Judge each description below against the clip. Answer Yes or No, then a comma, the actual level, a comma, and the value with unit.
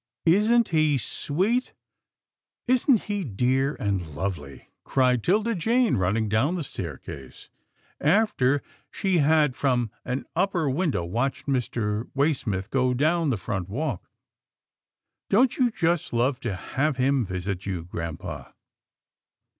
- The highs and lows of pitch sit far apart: Yes, wide, 8.4 semitones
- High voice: No, low, 135 Hz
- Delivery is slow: Yes, slow, 130 wpm